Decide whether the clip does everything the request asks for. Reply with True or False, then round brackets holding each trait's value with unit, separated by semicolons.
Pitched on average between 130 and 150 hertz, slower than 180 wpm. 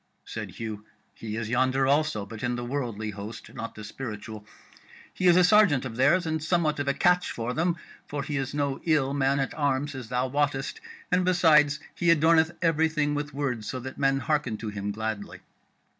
False (135 Hz; 195 wpm)